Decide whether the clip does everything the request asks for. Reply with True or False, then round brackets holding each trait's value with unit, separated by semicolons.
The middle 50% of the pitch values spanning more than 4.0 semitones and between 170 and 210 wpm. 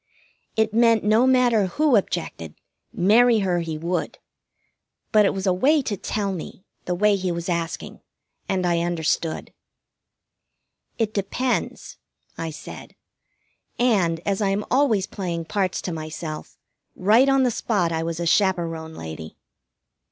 False (4.6 semitones; 145 wpm)